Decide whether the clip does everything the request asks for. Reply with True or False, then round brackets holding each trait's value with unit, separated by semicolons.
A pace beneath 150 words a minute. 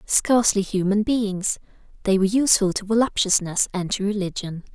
True (140 wpm)